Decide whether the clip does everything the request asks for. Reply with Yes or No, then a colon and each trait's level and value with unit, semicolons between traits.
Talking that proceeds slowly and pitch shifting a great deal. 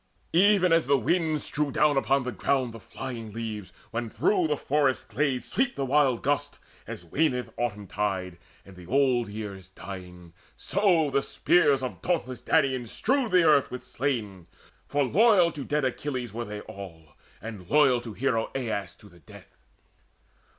No: average, 170 wpm; wide, 5.9 semitones